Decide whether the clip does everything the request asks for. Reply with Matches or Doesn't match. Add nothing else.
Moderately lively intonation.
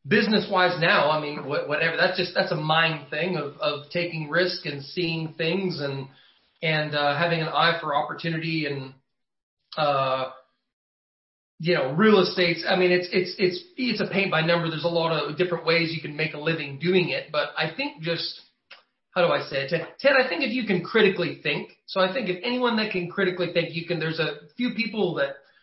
Matches